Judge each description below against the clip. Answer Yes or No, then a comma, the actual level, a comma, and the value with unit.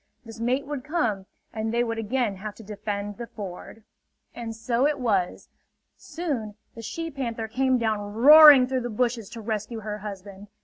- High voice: Yes, high, 225 Hz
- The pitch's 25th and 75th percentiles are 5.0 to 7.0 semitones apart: No, average, 3.2 semitones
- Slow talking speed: No, average, 175 wpm